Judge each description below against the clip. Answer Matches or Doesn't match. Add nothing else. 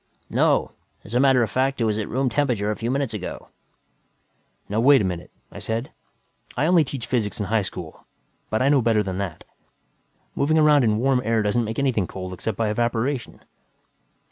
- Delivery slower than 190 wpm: Doesn't match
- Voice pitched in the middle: Doesn't match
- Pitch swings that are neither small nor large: Matches